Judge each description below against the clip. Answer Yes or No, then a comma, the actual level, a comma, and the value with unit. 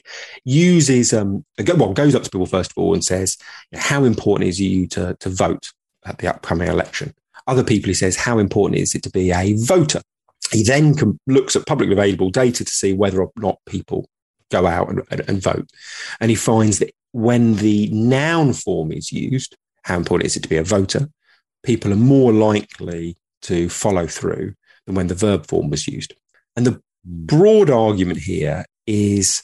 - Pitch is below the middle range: Yes, low, 105 Hz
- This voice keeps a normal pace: Yes, average, 190 wpm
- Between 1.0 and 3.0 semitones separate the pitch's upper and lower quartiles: No, average, 5.1 semitones